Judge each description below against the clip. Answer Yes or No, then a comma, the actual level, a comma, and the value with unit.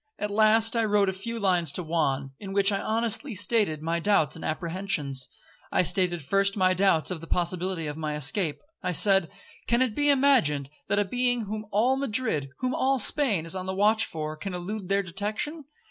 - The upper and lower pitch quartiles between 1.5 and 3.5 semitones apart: No, average, 4.8 semitones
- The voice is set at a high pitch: Yes, high, 195 Hz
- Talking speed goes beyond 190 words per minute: Yes, average, 200 wpm